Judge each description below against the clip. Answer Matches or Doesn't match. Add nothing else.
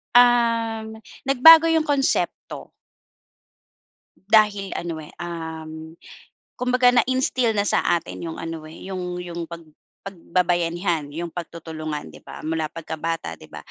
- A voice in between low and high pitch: Matches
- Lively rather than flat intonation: Matches